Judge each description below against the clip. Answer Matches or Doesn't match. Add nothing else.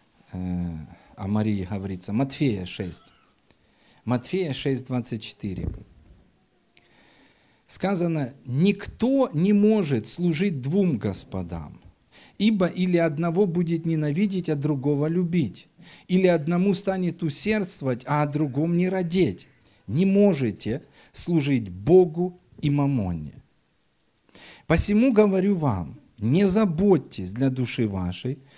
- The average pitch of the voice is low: Doesn't match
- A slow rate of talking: Matches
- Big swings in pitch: Matches